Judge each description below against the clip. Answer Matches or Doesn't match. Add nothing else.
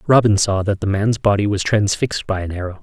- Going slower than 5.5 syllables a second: Doesn't match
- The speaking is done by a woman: Doesn't match